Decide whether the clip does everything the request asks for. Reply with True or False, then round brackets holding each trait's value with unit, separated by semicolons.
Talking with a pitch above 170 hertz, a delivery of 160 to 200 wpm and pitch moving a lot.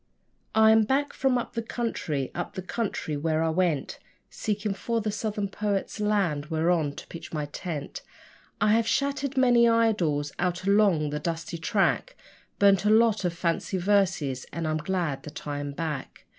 True (190 Hz; 170 wpm; 5.7 semitones)